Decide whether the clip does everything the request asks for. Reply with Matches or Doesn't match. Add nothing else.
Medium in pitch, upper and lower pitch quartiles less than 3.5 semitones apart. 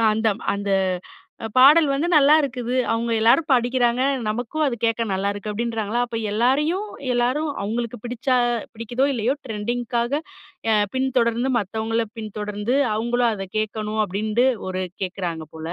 Doesn't match